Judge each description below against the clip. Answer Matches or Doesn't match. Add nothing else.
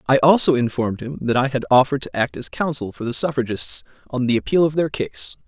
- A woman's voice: Doesn't match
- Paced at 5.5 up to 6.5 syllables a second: Matches